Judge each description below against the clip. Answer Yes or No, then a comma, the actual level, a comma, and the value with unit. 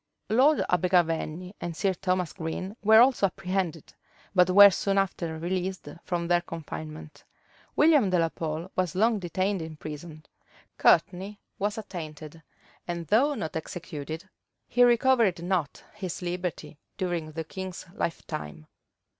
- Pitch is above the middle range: No, medium, 180 Hz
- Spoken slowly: Yes, slow, 130 wpm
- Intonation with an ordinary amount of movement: Yes, average, 3.4 semitones